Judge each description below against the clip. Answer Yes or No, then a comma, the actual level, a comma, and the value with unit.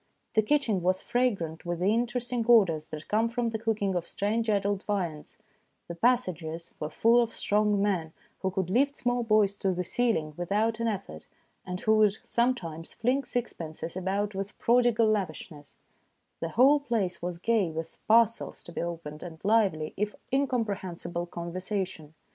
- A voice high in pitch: Yes, high, 200 Hz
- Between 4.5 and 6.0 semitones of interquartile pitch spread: Yes, average, 5.0 semitones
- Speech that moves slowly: No, average, 165 wpm